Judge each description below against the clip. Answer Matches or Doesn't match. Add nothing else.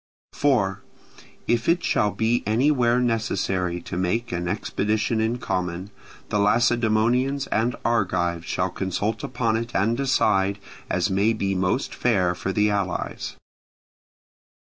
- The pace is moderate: Doesn't match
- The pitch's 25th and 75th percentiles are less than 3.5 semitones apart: Doesn't match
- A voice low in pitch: Matches